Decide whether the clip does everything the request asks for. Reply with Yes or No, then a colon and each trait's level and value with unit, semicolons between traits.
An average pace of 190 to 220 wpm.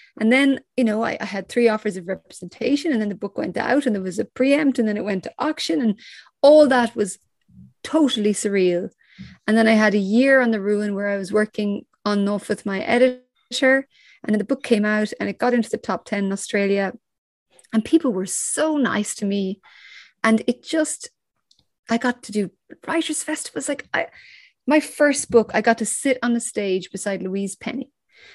Yes: fast, 205 wpm